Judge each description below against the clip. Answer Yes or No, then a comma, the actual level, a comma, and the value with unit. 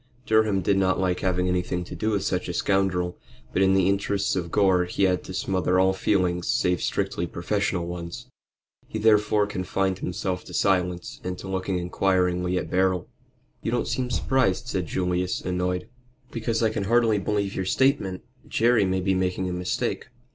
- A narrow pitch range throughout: Yes, narrow, 2.0 semitones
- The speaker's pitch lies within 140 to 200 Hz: No, very low, 95 Hz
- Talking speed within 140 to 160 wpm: No, average, 175 wpm